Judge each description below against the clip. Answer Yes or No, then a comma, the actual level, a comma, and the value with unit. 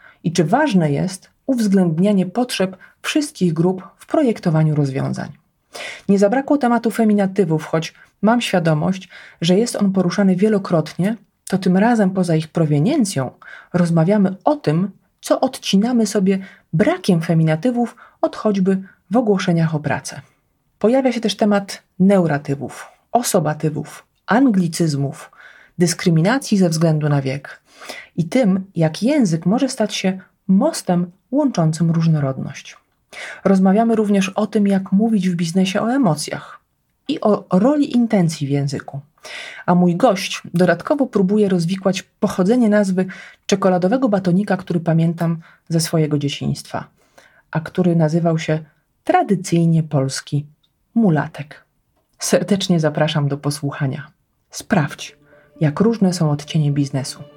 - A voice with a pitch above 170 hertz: Yes, medium, 185 Hz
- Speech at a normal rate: Yes, average, 120 wpm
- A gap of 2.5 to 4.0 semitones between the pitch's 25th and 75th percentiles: No, average, 4.6 semitones